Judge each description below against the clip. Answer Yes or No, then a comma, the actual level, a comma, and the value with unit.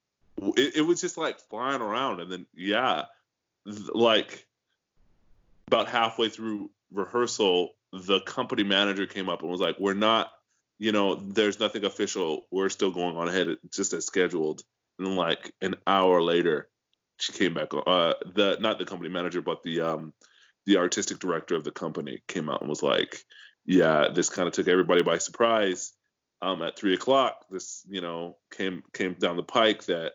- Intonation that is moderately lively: Yes, average, 3.7 semitones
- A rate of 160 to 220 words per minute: Yes, average, 175 wpm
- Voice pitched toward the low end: Yes, very low, 95 Hz